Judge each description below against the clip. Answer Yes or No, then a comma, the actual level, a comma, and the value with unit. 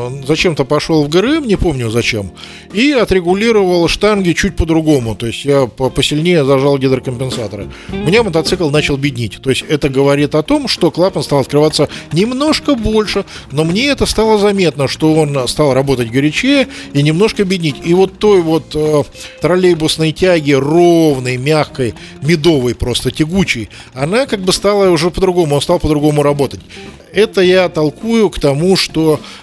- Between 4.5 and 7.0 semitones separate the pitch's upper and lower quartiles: Yes, average, 5.2 semitones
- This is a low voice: No, medium, 155 Hz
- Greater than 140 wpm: Yes, average, 155 wpm